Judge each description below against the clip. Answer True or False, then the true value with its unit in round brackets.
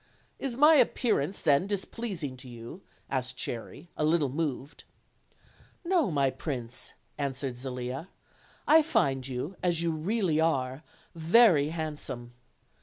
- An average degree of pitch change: False (6.2 semitones)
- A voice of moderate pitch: True (155 Hz)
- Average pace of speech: False (120 wpm)